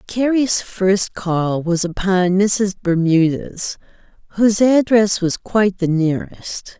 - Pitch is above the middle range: Yes, high, 195 Hz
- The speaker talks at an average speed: No, slow, 115 wpm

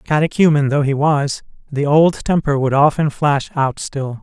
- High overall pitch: No, medium, 145 Hz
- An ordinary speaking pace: Yes, average, 170 wpm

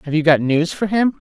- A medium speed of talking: No, fast, 280 wpm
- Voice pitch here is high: No, medium, 170 Hz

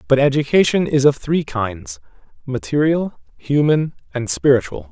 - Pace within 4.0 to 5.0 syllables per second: Yes, 4.6 syllables/s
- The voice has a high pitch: No, low, 135 Hz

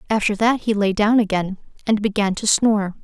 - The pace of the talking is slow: No, average, 200 wpm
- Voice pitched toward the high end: Yes, high, 210 Hz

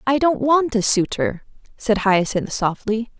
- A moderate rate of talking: Yes, average, 150 wpm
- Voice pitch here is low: No, high, 230 Hz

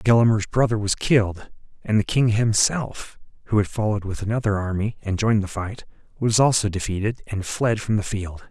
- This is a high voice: No, low, 105 Hz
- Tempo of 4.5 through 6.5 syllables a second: Yes, 5.4 syllables/s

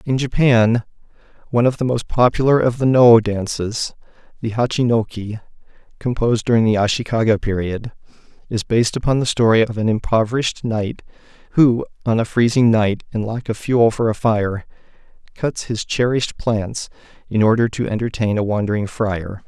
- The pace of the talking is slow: No, average, 155 wpm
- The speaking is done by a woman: No, male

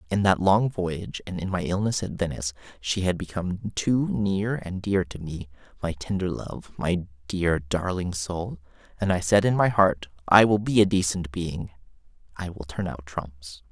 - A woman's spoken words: No, male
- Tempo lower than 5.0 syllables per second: Yes, 4.5 syllables/s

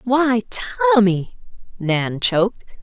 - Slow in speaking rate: Yes, slow, 85 wpm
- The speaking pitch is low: No, high, 220 Hz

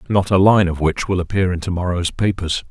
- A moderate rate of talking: No, fast, 245 wpm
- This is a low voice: Yes, very low, 90 Hz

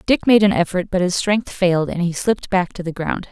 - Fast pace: Yes, fast, 270 wpm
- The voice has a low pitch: No, medium, 185 Hz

